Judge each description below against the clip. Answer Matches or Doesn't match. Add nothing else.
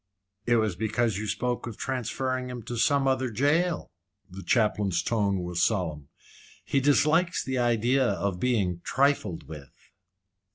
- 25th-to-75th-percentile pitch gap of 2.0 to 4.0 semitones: Doesn't match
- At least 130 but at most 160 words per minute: Matches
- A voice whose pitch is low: Matches